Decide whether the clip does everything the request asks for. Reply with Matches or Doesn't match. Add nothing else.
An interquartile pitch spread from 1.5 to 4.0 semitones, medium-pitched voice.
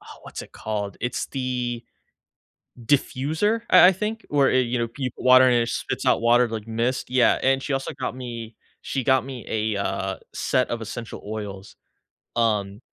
Doesn't match